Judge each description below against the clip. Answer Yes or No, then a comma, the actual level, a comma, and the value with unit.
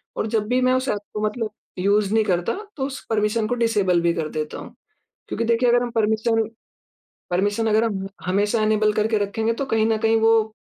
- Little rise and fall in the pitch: Yes, narrow, 1.8 semitones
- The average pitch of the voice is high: Yes, high, 220 Hz